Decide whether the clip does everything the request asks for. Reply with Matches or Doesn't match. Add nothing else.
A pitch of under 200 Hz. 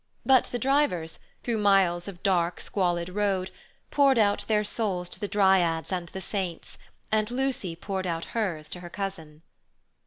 Matches